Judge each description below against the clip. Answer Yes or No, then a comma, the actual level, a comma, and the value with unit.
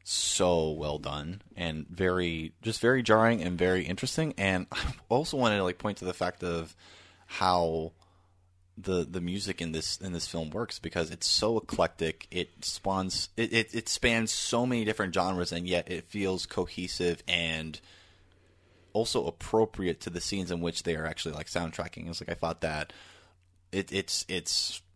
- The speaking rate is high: No, average, 175 wpm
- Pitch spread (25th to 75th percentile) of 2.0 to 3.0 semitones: Yes, narrow, 2.4 semitones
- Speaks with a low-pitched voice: Yes, very low, 90 Hz